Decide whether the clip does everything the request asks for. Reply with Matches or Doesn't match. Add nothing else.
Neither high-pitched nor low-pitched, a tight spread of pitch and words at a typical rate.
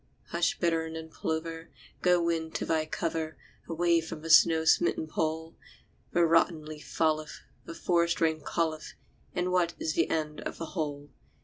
Matches